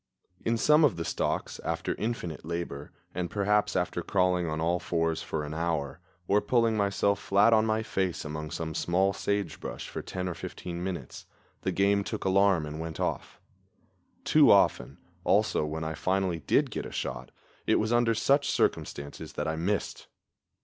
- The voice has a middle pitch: No, very low, 90 Hz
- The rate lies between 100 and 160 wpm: No, average, 170 wpm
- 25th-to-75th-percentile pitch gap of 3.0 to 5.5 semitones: Yes, average, 4.1 semitones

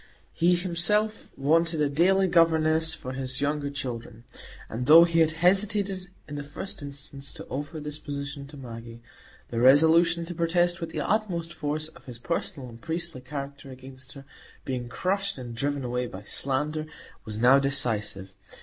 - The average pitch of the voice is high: No, medium, 145 Hz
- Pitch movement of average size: Yes, average, 4.3 semitones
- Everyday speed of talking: Yes, average, 165 wpm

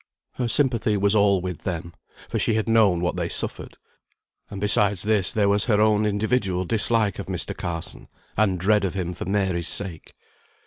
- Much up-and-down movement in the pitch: No, average, 2.8 semitones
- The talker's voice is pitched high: No, low, 100 Hz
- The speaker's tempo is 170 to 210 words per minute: Yes, average, 180 wpm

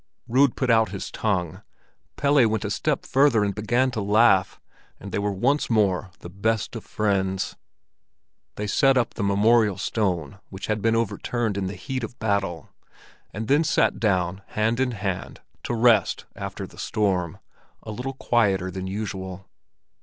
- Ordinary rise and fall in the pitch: Yes, average, 3.5 semitones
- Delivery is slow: No, average, 165 wpm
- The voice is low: Yes, low, 105 Hz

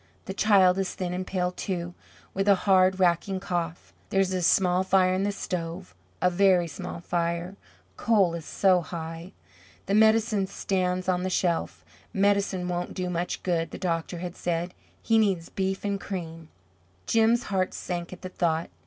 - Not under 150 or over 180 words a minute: Yes, average, 170 wpm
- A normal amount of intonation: No, narrow, 1.9 semitones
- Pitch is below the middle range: No, medium, 185 Hz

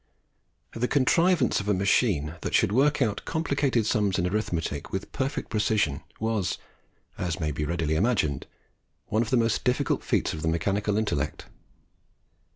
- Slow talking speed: No, average, 155 wpm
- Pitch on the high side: No, low, 105 Hz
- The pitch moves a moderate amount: No, wide, 6.6 semitones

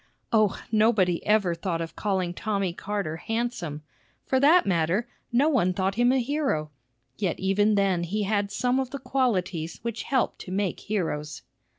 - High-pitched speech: Yes, high, 200 Hz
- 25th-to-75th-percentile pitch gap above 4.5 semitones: Yes, average, 4.9 semitones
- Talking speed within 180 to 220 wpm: No, average, 165 wpm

